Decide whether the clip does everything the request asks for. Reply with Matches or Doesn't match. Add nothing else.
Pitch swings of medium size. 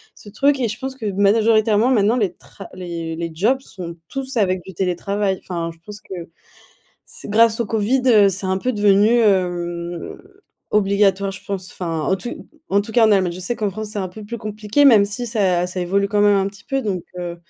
Matches